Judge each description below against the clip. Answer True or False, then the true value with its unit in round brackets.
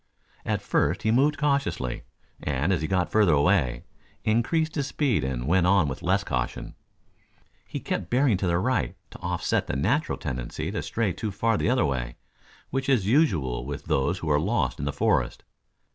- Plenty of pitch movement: True (8.6 semitones)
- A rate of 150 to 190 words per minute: True (185 wpm)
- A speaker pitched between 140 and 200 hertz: False (95 Hz)